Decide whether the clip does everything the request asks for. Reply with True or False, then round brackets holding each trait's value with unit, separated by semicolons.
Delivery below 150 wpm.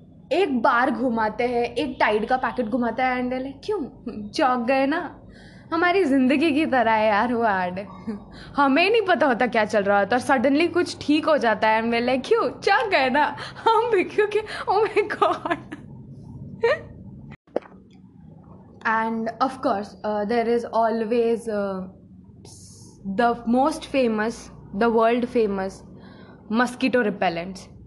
True (135 wpm)